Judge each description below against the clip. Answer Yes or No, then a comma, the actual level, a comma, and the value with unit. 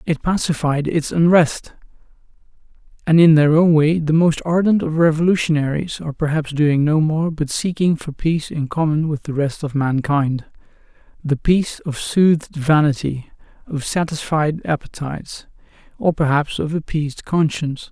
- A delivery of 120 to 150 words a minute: Yes, average, 140 wpm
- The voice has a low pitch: No, medium, 155 Hz